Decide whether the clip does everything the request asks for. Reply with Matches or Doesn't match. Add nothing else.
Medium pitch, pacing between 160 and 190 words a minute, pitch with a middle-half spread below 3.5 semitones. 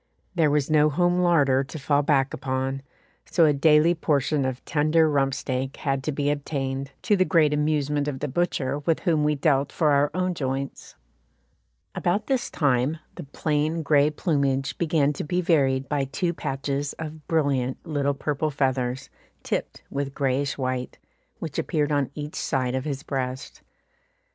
Matches